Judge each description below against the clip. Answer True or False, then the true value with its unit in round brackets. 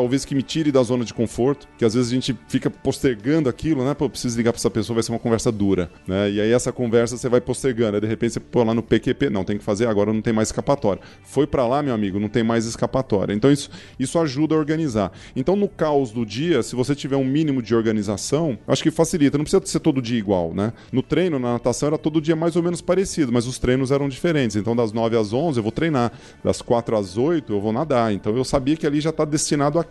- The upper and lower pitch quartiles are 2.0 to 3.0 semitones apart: False (4.3 semitones)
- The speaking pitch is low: True (125 Hz)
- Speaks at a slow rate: False (265 wpm)